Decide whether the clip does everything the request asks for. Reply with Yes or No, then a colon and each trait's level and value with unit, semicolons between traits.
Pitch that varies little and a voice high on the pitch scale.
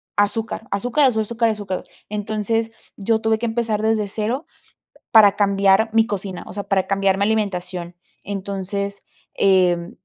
Yes: narrow, 2.2 semitones; high, 205 Hz